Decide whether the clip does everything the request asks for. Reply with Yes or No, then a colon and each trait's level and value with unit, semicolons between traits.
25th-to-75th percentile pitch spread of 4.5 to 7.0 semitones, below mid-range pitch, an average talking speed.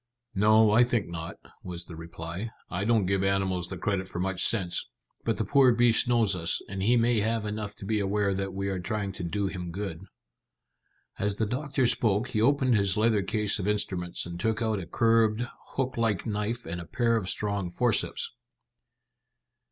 No: average, 3.3 semitones; low, 105 Hz; average, 190 wpm